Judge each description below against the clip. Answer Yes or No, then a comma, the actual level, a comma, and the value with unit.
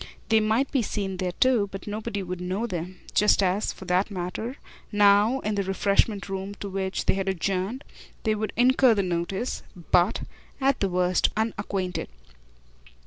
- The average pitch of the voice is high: Yes, high, 200 Hz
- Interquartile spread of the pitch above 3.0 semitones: No, average, 2.7 semitones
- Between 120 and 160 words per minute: No, average, 175 wpm